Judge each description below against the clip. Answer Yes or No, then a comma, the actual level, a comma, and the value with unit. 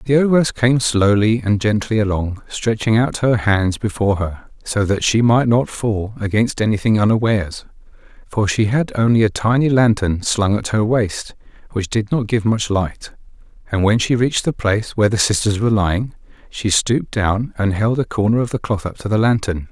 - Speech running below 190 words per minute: No, average, 195 wpm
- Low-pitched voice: Yes, low, 110 Hz